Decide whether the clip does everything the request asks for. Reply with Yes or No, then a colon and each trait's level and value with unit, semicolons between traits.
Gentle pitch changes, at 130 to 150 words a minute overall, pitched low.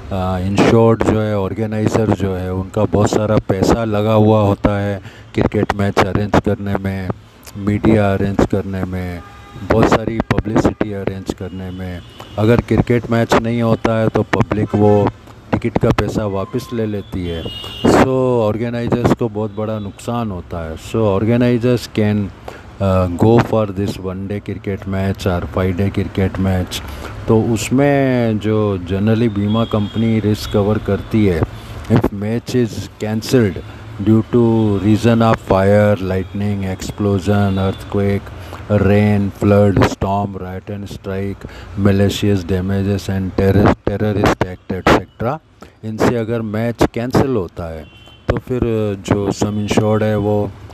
Yes: narrow, 2.2 semitones; average, 135 wpm; low, 105 Hz